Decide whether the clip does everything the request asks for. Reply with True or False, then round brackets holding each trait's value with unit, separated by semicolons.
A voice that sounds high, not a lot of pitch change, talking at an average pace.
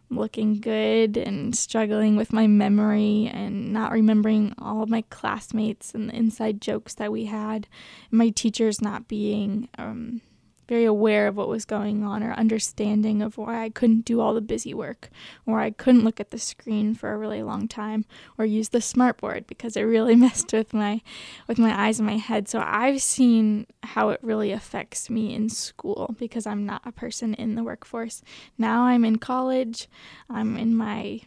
True (220 Hz; 1.3 semitones; 190 wpm)